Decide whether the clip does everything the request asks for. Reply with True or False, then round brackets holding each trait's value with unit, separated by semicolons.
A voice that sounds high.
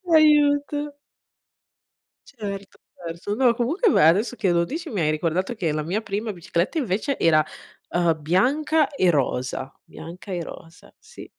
True (200 Hz)